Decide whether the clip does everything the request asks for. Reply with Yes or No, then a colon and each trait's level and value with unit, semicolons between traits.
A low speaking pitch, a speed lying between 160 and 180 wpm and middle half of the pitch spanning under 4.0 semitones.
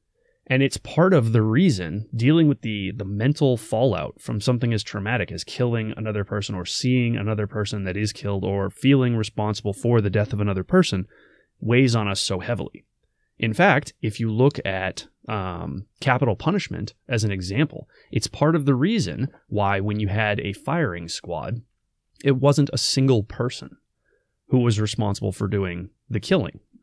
No: low, 110 Hz; average, 170 wpm; average, 4.7 semitones